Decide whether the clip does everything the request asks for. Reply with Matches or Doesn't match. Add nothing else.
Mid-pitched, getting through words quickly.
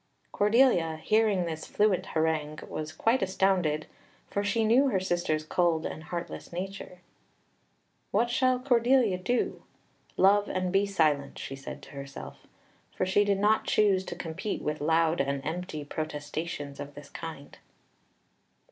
Doesn't match